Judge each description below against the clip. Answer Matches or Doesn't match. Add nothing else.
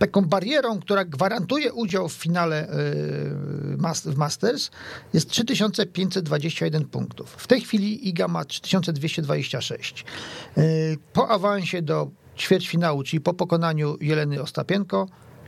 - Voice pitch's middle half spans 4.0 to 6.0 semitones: Matches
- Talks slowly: Matches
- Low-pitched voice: Doesn't match